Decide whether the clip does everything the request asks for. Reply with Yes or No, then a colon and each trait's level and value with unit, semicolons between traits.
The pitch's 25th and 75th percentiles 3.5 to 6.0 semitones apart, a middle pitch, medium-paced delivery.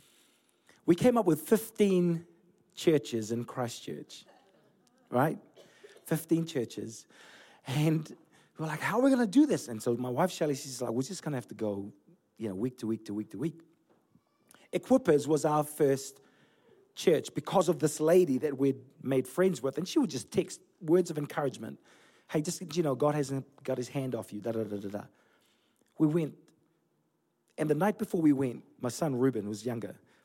Yes: average, 5.2 semitones; medium, 150 Hz; average, 190 wpm